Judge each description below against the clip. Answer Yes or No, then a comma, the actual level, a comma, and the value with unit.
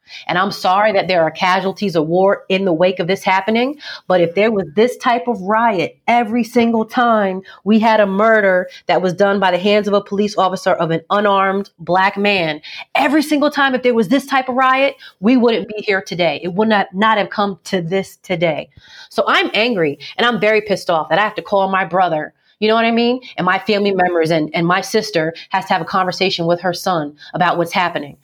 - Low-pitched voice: No, high, 195 Hz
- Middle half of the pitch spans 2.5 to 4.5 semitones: Yes, average, 3.4 semitones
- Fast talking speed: Yes, fast, 230 wpm